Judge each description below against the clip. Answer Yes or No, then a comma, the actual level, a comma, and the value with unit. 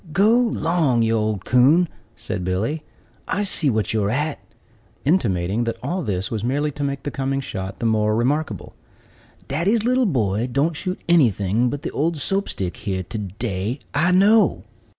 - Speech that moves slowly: No, average, 170 wpm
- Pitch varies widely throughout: Yes, wide, 7.4 semitones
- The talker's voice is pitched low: Yes, low, 130 Hz